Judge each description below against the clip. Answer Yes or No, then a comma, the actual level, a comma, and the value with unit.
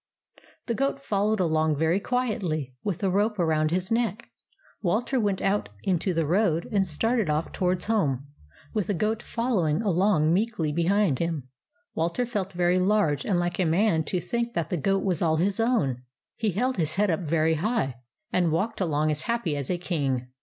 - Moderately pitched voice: Yes, medium, 180 Hz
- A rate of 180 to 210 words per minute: Yes, average, 190 wpm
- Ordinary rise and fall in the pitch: Yes, average, 4.9 semitones